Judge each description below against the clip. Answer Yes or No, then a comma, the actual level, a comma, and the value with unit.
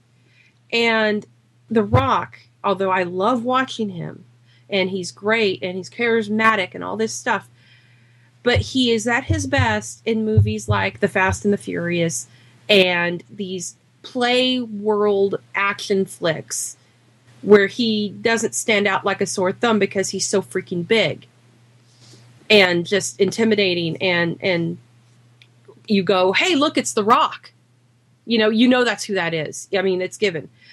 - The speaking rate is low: No, average, 150 wpm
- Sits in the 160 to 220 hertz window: Yes, high, 190 Hz